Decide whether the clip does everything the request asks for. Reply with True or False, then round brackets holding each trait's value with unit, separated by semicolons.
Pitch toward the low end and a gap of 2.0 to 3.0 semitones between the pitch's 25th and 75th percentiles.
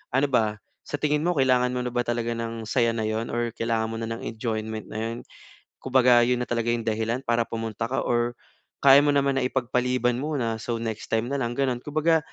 True (120 Hz; 2.5 semitones)